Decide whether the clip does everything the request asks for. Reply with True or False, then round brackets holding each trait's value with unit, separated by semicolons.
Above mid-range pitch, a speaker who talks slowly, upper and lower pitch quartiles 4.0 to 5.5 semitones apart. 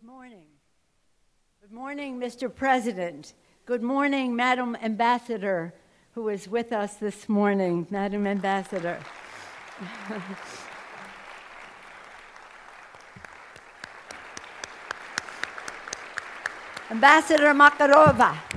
True (230 Hz; 65 wpm; 4.4 semitones)